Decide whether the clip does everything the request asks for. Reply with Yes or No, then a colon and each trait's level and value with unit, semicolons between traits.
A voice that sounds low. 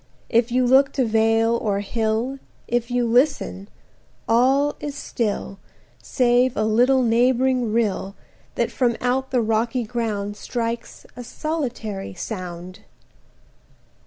No: high, 235 Hz